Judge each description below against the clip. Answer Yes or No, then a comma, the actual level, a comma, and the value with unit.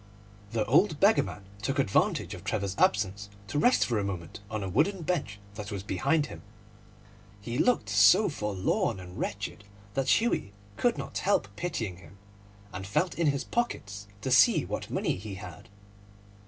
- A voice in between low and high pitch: No, low, 105 Hz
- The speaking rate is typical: Yes, average, 170 wpm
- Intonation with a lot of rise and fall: Yes, wide, 6.7 semitones